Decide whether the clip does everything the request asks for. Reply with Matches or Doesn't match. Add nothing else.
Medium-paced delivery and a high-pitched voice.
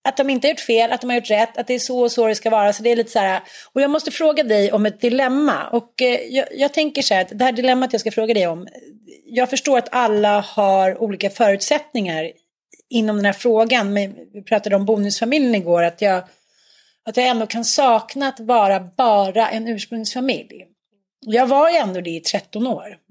Doesn't match